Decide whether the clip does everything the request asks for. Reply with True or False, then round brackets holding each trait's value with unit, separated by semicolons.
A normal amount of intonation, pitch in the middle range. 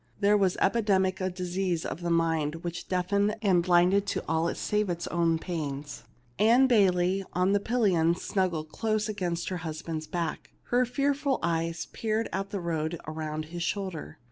True (3.4 semitones; 180 Hz)